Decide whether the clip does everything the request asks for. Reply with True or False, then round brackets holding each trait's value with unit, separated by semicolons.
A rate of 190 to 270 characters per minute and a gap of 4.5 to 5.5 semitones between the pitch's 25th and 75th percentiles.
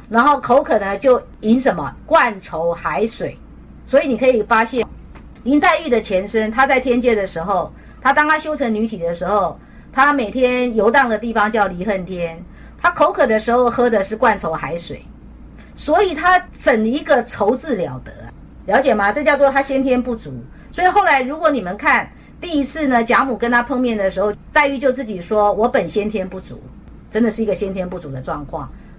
False (280 characters per minute; 5.1 semitones)